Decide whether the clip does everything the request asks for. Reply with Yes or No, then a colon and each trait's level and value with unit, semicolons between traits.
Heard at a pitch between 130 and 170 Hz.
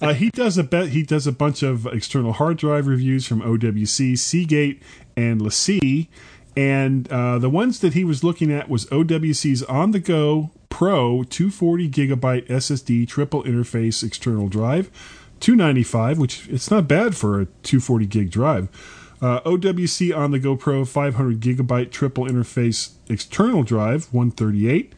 Yes: low, 135 Hz